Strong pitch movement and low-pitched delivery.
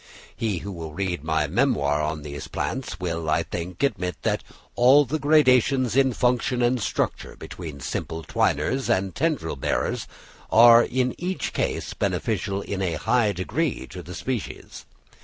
Yes: wide, 7.6 semitones; low, 100 Hz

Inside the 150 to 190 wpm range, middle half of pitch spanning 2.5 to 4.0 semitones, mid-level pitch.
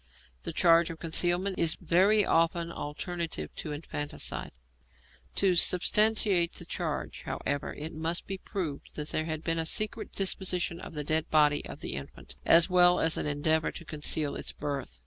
Yes: average, 165 wpm; average, 2.8 semitones; medium, 165 Hz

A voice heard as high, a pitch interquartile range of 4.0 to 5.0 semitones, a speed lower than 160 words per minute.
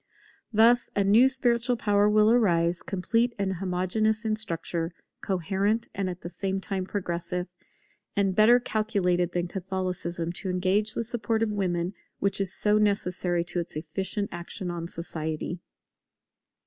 No: high, 195 Hz; average, 3.3 semitones; average, 145 wpm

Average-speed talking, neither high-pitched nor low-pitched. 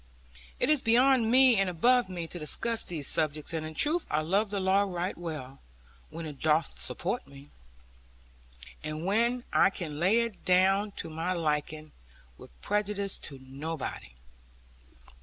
Yes: average, 155 wpm; medium, 180 Hz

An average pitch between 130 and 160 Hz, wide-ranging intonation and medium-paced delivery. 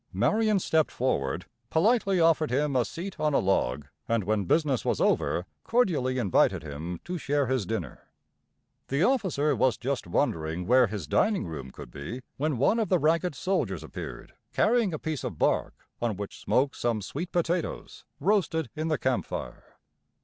Yes: medium, 140 Hz; wide, 8.0 semitones; average, 170 wpm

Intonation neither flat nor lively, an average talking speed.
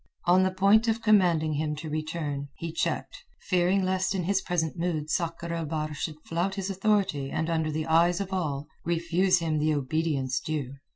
Yes: average, 3.3 semitones; average, 185 wpm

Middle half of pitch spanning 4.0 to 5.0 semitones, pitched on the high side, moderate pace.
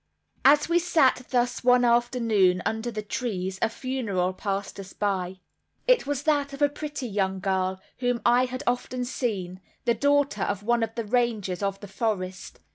Yes: average, 4.7 semitones; high, 230 Hz; average, 175 wpm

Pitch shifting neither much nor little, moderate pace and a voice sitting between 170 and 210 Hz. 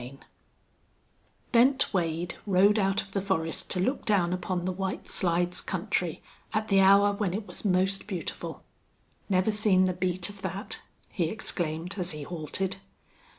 No: narrow, 2.3 semitones; average, 160 wpm; medium, 185 Hz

